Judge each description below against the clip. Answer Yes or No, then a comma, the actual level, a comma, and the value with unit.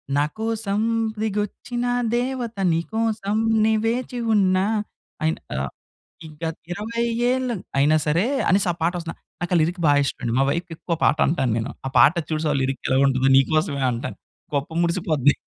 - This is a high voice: No, medium, 170 Hz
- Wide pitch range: Yes, wide, 6.8 semitones